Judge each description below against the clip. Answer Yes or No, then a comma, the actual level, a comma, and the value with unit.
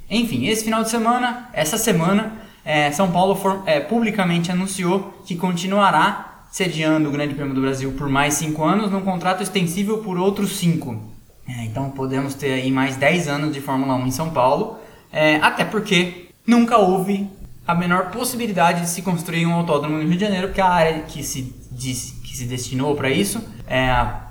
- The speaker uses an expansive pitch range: Yes, wide, 5.9 semitones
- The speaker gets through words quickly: Yes, fast, 190 wpm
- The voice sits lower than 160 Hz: No, medium, 170 Hz